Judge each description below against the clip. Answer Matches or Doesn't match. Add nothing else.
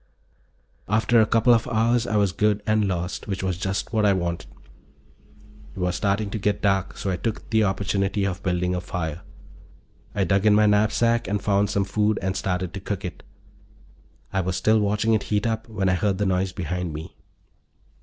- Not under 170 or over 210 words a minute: Matches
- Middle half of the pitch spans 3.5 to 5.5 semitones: Doesn't match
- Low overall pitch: Matches